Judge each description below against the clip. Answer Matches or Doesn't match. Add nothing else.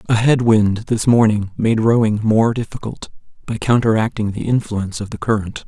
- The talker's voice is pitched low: Matches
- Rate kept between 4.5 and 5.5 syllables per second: Matches